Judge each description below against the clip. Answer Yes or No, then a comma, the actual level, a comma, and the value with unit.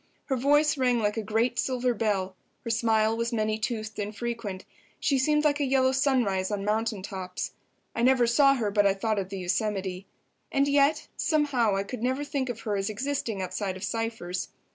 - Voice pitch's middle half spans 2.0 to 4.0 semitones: No, average, 4.4 semitones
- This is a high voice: Yes, high, 225 Hz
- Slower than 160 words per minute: No, average, 195 wpm